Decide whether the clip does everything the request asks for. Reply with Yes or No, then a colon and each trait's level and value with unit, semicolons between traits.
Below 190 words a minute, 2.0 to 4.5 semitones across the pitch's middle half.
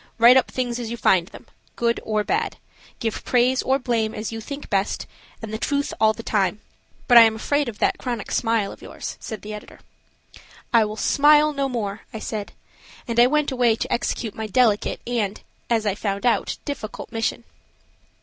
No: average, 195 wpm; average, 2.8 semitones